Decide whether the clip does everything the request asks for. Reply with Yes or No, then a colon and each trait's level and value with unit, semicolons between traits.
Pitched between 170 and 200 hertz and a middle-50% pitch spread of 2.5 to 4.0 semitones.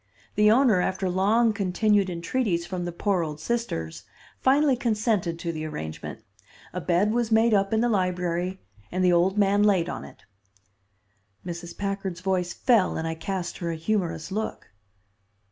Yes: high, 190 Hz; average, 3.7 semitones